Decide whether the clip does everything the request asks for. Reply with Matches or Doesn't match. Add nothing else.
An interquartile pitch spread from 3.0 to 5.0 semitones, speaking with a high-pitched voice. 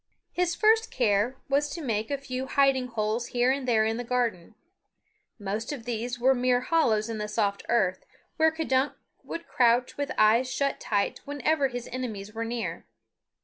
Matches